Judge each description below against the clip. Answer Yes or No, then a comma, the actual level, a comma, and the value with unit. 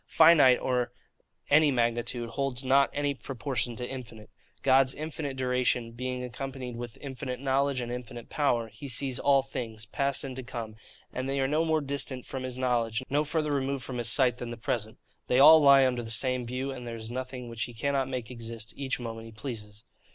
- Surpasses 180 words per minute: Yes, average, 200 wpm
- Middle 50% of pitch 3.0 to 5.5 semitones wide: No, narrow, 2.5 semitones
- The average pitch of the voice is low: Yes, low, 130 Hz